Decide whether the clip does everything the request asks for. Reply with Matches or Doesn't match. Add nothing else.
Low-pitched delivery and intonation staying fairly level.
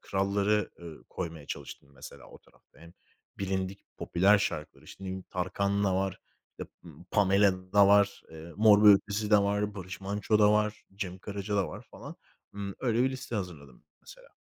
Matches